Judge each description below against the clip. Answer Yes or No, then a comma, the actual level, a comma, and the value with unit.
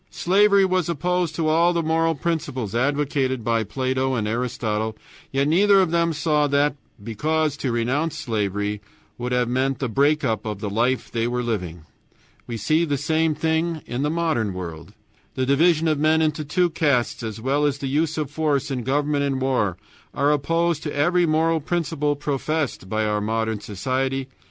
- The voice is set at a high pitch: No, medium, 140 Hz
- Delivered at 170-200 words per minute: Yes, average, 180 wpm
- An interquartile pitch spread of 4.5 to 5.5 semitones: Yes, average, 5.1 semitones